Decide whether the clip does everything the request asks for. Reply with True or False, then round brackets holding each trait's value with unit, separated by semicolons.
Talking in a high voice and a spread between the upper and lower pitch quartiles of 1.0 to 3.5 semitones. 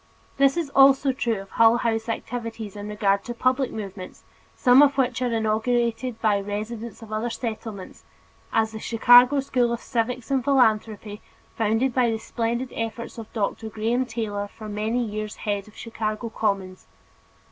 True (225 Hz; 2.4 semitones)